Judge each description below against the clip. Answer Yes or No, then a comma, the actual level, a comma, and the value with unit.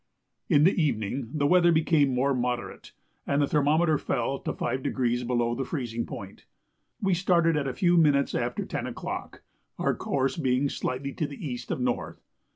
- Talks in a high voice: No, medium, 140 Hz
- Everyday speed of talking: Yes, average, 170 wpm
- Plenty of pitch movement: No, average, 4.0 semitones